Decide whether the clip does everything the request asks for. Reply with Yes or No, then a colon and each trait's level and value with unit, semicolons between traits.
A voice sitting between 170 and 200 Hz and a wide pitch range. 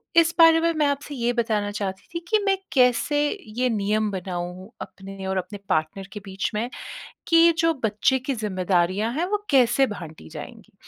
No: high, 215 Hz; wide, 6.8 semitones